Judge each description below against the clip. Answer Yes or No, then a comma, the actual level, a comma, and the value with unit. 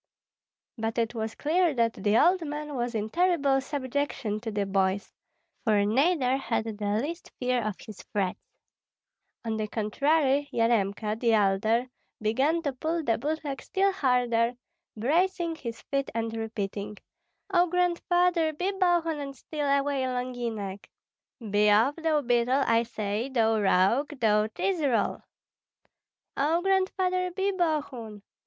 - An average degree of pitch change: No, wide, 6.2 semitones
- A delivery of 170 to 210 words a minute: No, average, 140 wpm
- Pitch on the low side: No, very high, 255 Hz